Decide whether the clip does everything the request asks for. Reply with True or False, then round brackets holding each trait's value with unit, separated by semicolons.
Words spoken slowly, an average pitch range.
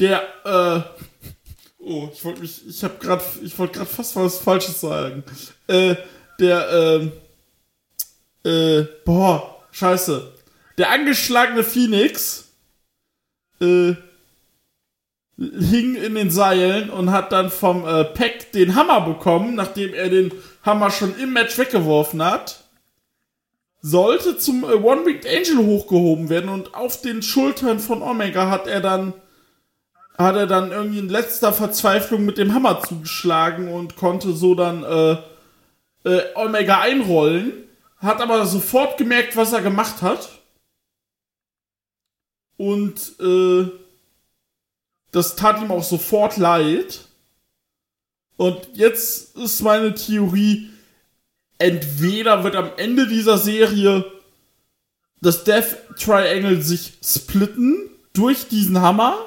True (120 wpm; 4.0 semitones)